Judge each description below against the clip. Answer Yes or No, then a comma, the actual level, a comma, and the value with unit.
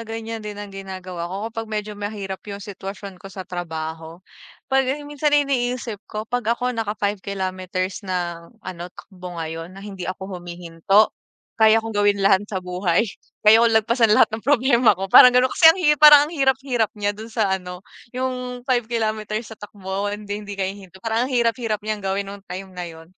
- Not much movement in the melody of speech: No, average, 3.5 semitones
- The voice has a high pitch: Yes, high, 205 Hz